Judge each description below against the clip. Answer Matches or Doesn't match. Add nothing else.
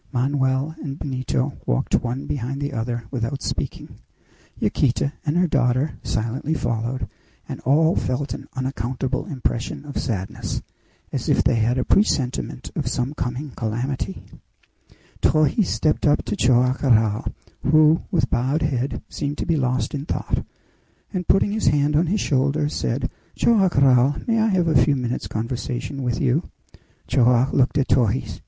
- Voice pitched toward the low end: Matches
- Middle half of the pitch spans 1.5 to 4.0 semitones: Matches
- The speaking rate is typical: Matches